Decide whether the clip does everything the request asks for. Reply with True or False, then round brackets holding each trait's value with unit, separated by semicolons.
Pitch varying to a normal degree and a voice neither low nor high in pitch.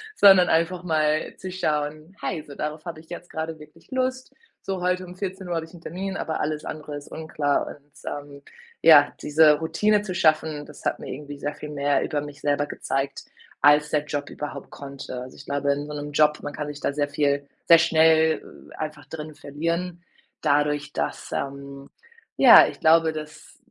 False (2.2 semitones; 150 Hz)